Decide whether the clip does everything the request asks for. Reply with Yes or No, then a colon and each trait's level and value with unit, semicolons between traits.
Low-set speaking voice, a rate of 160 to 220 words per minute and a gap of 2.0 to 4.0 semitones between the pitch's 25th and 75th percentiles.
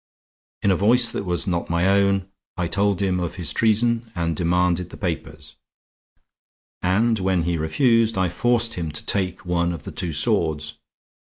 Yes: very low, 90 Hz; average, 170 wpm; average, 3.3 semitones